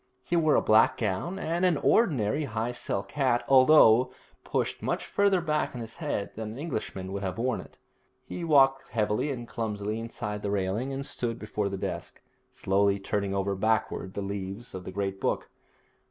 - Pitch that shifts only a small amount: No, average, 5.3 semitones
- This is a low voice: Yes, low, 110 Hz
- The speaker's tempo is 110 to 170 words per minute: No, average, 185 wpm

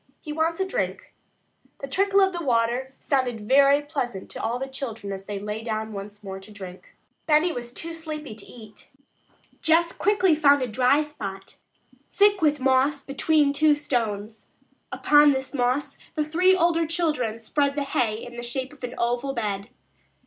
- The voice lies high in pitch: Yes, very high, 270 Hz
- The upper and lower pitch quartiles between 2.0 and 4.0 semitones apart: No, average, 5.2 semitones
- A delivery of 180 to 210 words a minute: No, average, 170 wpm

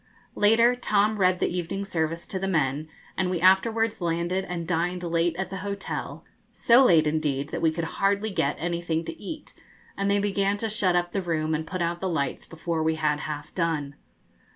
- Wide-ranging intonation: No, average, 3.6 semitones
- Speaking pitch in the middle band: Yes, medium, 175 Hz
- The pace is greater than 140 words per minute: Yes, average, 200 wpm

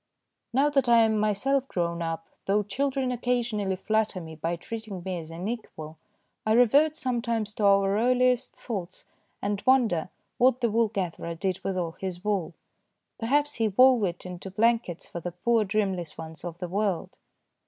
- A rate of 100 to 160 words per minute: No, average, 170 wpm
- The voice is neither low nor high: No, high, 210 Hz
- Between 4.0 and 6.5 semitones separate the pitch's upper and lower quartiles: Yes, average, 5.0 semitones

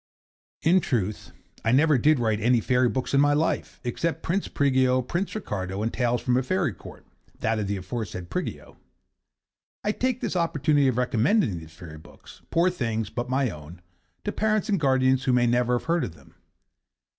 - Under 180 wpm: No, average, 185 wpm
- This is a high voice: No, low, 125 Hz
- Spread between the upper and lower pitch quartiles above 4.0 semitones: Yes, wide, 5.6 semitones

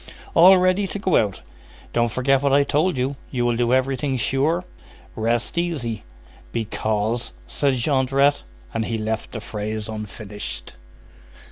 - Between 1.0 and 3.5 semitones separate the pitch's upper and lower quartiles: No, average, 4.3 semitones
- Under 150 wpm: Yes, average, 140 wpm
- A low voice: Yes, low, 125 Hz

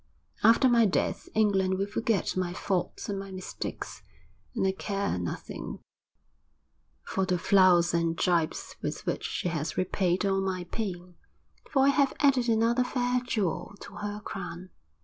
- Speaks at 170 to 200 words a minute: No, average, 150 wpm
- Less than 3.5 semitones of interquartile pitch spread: No, average, 3.9 semitones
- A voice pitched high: Yes, high, 195 Hz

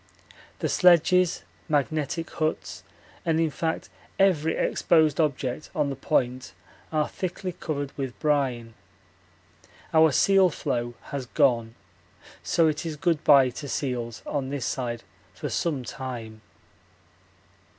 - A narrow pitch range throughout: No, average, 4.0 semitones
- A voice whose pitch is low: No, medium, 145 Hz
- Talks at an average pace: No, slow, 120 wpm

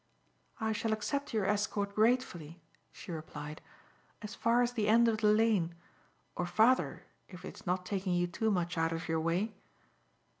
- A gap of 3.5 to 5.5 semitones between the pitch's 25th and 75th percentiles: Yes, average, 4.1 semitones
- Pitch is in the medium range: No, high, 205 Hz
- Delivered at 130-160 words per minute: No, average, 175 wpm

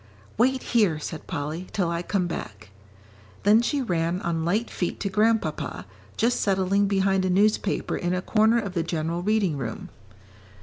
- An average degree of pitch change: Yes, average, 4.1 semitones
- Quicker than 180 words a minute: No, average, 165 wpm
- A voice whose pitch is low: No, medium, 185 Hz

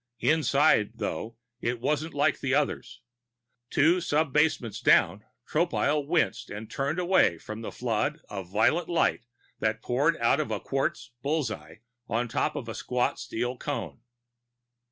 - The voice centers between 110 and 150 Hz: Yes, low, 135 Hz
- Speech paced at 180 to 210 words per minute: No, average, 150 wpm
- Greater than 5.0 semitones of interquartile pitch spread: Yes, wide, 5.4 semitones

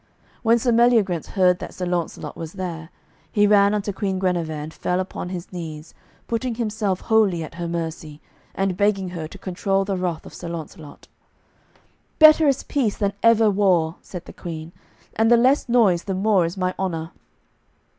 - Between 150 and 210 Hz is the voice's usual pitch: Yes, medium, 185 Hz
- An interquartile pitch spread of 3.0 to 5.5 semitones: Yes, average, 3.8 semitones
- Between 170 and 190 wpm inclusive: Yes, average, 175 wpm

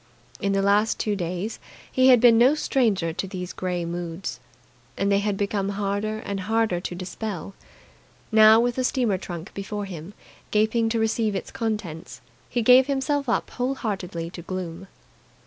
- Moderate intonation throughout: Yes, average, 3.7 semitones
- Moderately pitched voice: No, high, 205 Hz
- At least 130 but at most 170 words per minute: Yes, average, 165 wpm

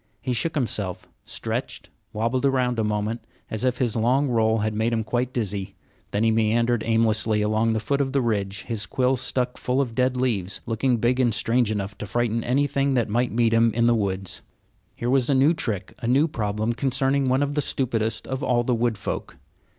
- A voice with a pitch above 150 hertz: No, low, 115 Hz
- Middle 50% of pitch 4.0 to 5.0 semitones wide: No, average, 2.9 semitones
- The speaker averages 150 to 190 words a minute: No, fast, 205 wpm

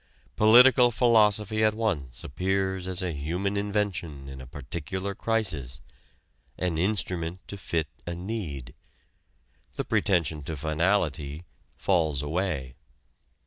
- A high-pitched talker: No, very low, 90 Hz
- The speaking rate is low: Yes, slow, 110 wpm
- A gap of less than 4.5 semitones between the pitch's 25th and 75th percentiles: No, average, 5.2 semitones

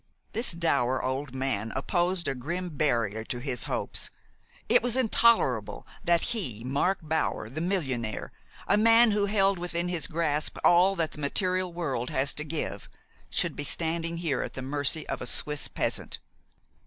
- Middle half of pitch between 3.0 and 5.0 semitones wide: No, wide, 5.4 semitones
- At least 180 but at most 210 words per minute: No, average, 165 wpm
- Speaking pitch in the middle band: Yes, medium, 160 Hz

